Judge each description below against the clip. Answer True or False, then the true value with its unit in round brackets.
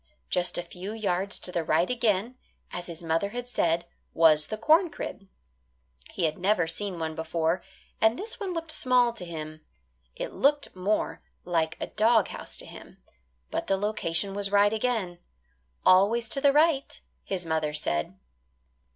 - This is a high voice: True (195 Hz)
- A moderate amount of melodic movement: False (5.7 semitones)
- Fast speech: False (165 wpm)